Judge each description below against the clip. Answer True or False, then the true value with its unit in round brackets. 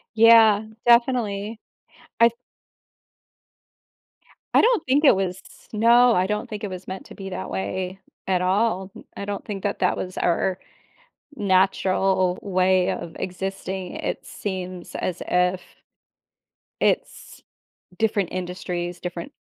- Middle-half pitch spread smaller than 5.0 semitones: True (2.5 semitones)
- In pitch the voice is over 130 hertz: True (190 Hz)